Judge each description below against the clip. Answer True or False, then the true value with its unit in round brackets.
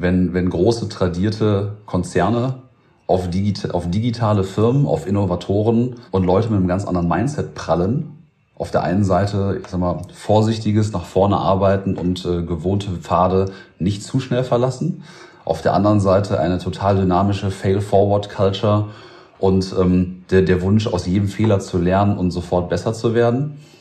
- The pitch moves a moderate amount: True (3.2 semitones)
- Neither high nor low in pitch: False (100 Hz)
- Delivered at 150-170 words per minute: True (160 wpm)